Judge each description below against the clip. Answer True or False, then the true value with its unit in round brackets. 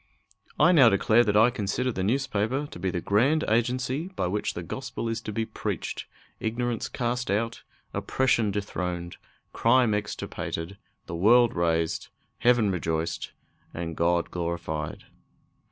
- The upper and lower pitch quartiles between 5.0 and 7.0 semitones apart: True (5.6 semitones)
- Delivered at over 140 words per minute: False (135 wpm)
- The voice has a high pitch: False (105 Hz)